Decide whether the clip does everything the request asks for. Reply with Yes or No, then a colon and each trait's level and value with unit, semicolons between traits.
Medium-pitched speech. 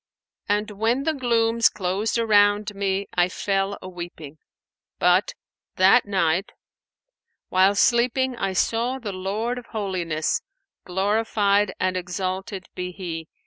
No: high, 200 Hz